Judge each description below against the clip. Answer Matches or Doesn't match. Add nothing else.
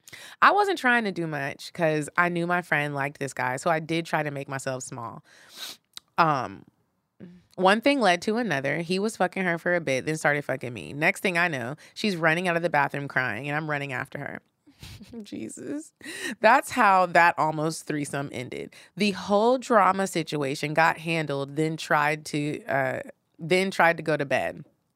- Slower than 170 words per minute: Doesn't match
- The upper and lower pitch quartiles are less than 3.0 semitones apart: Doesn't match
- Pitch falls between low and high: Matches